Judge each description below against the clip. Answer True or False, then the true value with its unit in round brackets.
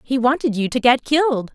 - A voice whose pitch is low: False (250 Hz)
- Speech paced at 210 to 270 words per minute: True (235 wpm)